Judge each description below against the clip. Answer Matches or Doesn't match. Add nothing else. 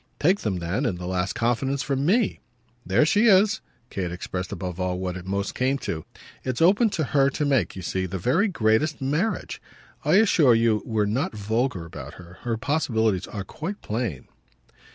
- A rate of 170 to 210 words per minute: Matches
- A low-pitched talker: Matches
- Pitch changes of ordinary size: Doesn't match